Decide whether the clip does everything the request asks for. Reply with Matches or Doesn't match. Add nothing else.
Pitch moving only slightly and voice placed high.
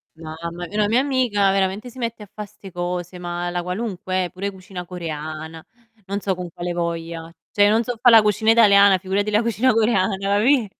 Doesn't match